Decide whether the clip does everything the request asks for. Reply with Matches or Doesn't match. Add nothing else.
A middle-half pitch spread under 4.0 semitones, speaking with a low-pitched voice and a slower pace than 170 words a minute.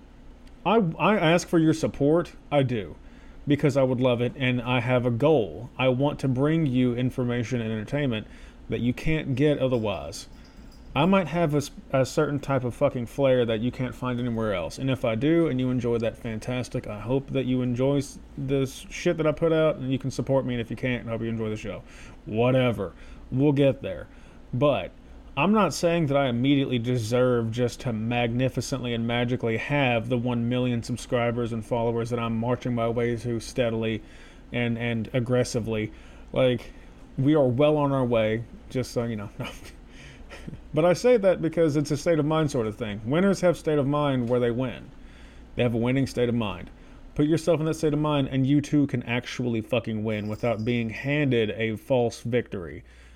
Doesn't match